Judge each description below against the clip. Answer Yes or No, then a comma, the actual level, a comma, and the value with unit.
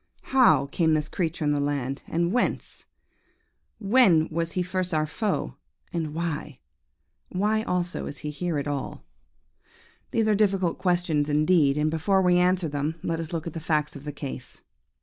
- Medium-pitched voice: Yes, medium, 165 Hz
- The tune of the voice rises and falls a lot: No, average, 3.4 semitones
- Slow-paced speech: No, average, 170 wpm